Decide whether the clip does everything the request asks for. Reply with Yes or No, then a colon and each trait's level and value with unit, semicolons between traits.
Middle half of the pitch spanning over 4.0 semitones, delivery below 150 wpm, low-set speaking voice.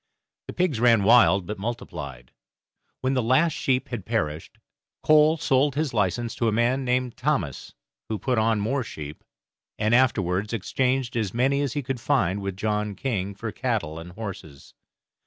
No: average, 4.8 semitones; average, 165 wpm; low, 115 Hz